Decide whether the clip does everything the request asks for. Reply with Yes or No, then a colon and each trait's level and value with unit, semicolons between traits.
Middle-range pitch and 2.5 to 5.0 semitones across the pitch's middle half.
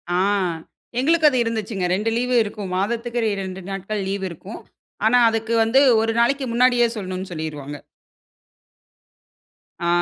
No: high, 220 Hz; average, 3.9 semitones